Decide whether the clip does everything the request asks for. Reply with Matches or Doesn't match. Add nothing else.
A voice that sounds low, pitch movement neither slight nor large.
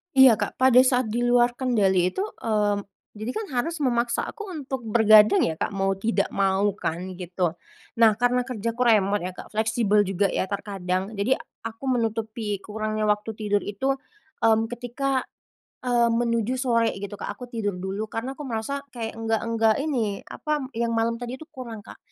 Doesn't match